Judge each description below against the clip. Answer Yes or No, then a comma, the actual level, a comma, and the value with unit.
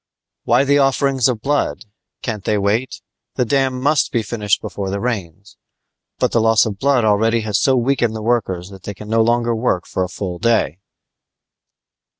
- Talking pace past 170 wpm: Yes, average, 180 wpm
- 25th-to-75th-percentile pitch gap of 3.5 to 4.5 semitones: Yes, average, 3.9 semitones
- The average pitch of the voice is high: No, low, 115 Hz